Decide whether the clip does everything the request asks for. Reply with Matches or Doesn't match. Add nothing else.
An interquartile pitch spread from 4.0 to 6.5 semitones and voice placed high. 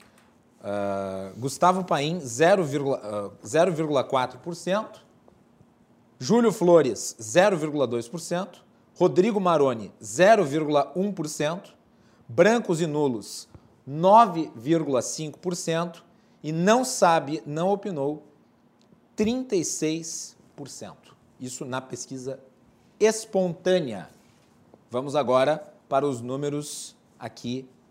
Doesn't match